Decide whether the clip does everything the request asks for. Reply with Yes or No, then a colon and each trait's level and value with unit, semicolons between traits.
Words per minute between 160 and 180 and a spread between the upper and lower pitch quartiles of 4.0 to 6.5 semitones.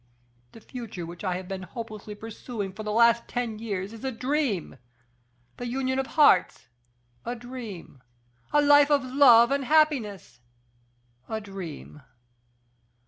No: average, 140 wpm; average, 4.9 semitones